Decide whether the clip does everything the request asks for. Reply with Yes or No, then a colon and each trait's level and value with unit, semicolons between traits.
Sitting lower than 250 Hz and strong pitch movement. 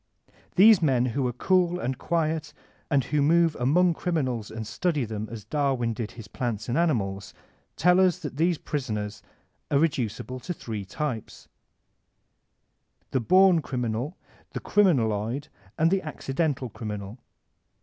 Yes: low, 135 Hz; wide, 6.5 semitones